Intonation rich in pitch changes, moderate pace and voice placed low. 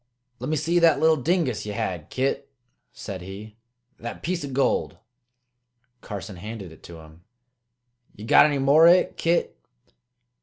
Yes: wide, 8.1 semitones; average, 155 wpm; low, 130 Hz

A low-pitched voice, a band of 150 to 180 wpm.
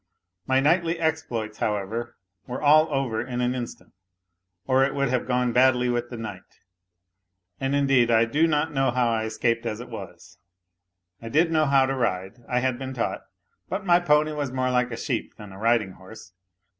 No: low, 125 Hz; average, 190 wpm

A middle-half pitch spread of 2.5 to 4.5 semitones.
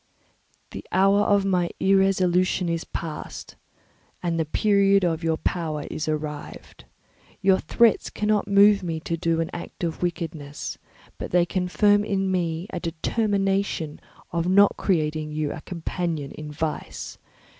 Yes: average, 3.4 semitones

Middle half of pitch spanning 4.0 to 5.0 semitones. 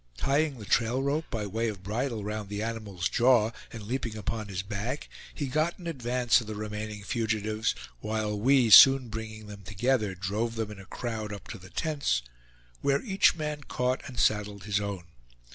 No: average, 3.5 semitones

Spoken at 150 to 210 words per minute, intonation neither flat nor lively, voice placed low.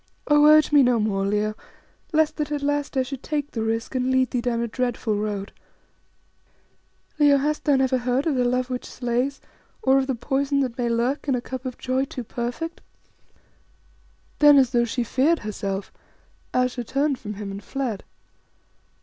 No: average, 185 wpm; average, 3.1 semitones; very high, 255 Hz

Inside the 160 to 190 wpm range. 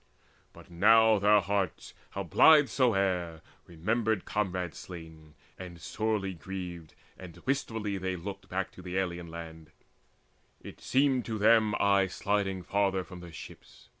No: slow, 135 wpm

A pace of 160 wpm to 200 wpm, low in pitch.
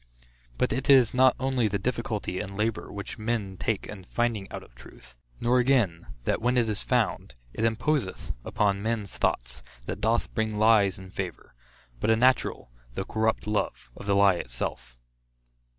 Yes: average, 170 wpm; low, 110 Hz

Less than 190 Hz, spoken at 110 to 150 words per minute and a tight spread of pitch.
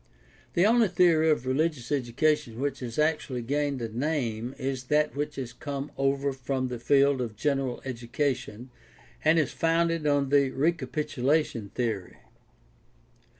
No: medium, 140 Hz; average, 145 wpm; average, 3.4 semitones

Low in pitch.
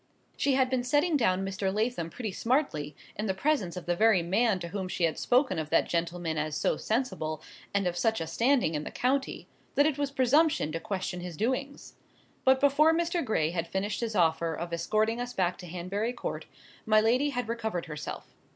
No: high, 210 Hz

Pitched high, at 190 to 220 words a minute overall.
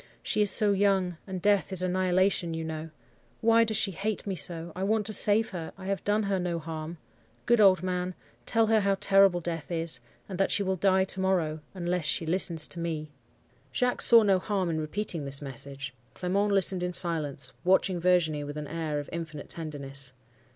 No: medium, 180 Hz; average, 200 wpm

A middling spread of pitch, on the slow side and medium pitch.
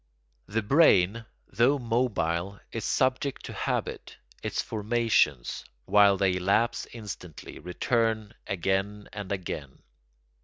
No: average, 3.8 semitones; slow, 105 wpm; low, 105 Hz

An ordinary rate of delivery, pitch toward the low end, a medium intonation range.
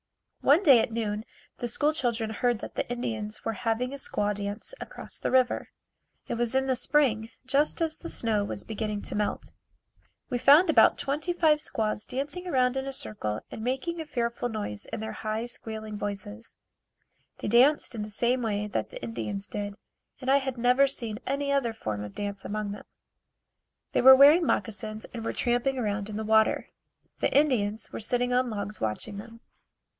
No: average, 190 wpm; high, 230 Hz; average, 4.0 semitones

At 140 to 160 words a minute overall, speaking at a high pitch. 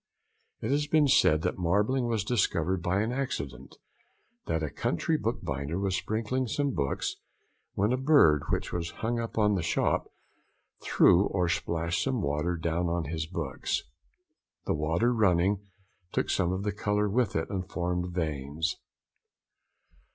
No: average, 150 wpm; very low, 90 Hz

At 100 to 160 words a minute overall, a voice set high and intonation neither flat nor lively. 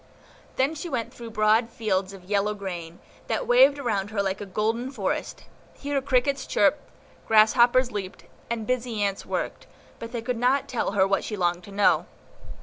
No: average, 175 wpm; high, 225 Hz; average, 4.2 semitones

